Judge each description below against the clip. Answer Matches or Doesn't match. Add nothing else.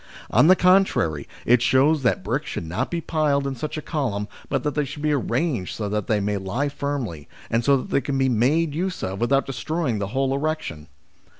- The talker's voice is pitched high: Doesn't match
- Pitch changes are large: Matches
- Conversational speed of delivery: Doesn't match